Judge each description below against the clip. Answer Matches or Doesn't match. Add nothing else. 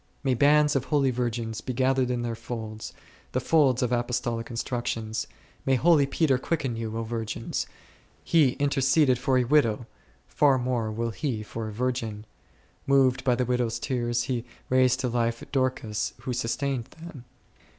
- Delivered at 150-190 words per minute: Matches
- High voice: Doesn't match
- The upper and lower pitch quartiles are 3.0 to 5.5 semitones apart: Doesn't match